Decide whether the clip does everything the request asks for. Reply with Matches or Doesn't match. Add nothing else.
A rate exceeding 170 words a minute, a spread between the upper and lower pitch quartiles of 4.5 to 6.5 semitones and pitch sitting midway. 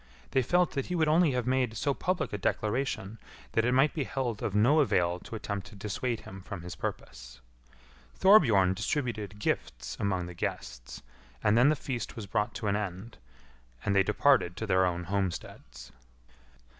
Doesn't match